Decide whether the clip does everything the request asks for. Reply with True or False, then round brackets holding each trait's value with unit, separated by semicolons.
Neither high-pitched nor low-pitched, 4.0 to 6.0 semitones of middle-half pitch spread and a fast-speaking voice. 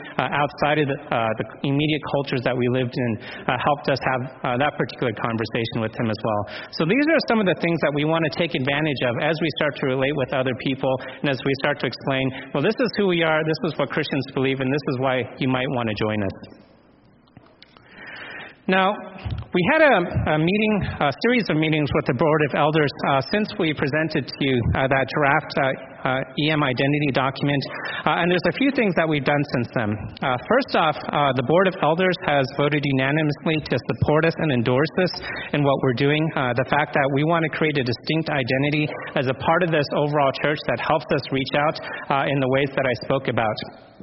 False (145 Hz; 3.2 semitones; 225 wpm)